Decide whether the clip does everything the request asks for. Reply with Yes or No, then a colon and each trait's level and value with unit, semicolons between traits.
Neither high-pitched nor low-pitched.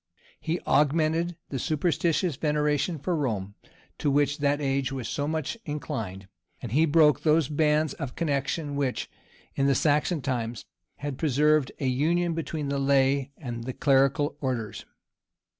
Yes: medium, 145 Hz